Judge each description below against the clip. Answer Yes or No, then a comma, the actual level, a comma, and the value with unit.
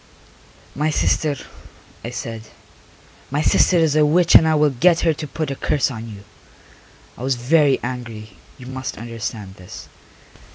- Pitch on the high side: No, low, 130 Hz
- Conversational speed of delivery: Yes, average, 160 wpm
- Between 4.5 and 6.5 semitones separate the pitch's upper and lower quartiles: Yes, average, 4.8 semitones